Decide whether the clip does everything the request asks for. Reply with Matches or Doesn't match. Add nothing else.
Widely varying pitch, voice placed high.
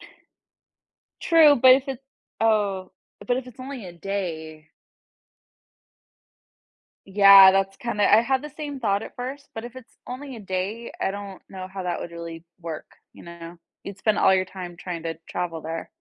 Matches